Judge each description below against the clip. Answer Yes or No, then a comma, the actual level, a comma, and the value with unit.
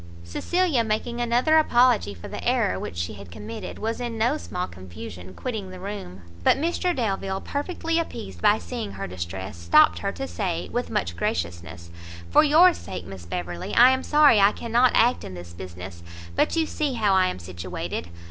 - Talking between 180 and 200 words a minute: Yes, average, 185 wpm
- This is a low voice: No, high, 190 Hz